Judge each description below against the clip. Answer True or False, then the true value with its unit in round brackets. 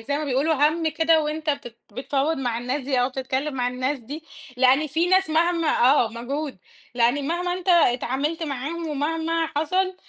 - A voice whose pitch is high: True (295 Hz)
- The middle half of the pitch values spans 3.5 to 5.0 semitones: True (3.8 semitones)